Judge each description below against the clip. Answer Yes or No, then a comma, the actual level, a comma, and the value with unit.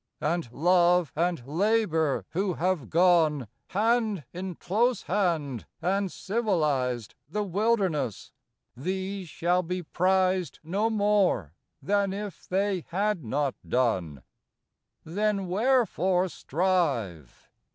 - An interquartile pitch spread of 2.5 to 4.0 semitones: No, average, 4.5 semitones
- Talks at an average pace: No, slow, 100 wpm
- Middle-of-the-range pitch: Yes, medium, 180 Hz